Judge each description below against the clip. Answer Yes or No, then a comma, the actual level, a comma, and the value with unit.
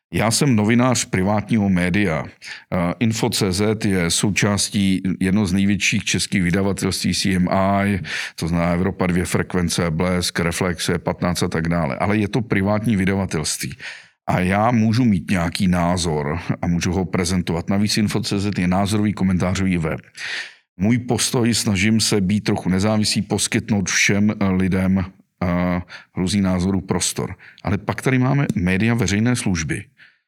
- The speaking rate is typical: Yes, average, 135 wpm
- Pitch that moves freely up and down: No, average, 2.8 semitones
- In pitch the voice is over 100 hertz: No, very low, 95 Hz